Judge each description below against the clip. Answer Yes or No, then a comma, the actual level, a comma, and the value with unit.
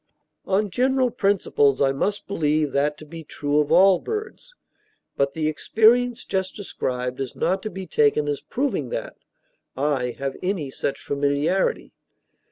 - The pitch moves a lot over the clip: Yes, wide, 6.4 semitones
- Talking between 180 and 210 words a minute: No, average, 150 wpm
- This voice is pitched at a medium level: Yes, medium, 160 Hz